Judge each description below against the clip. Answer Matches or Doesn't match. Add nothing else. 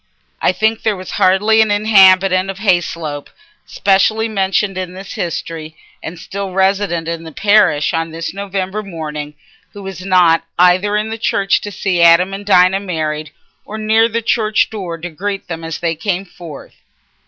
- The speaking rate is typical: Matches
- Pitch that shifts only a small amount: Doesn't match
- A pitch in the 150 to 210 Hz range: Matches